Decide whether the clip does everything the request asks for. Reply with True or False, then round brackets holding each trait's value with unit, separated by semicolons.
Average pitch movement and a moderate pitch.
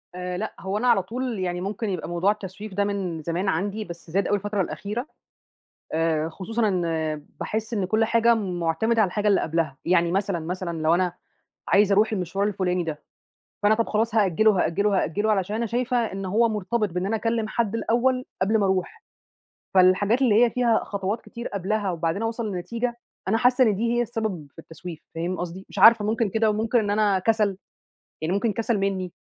False (3.6 semitones; 200 Hz)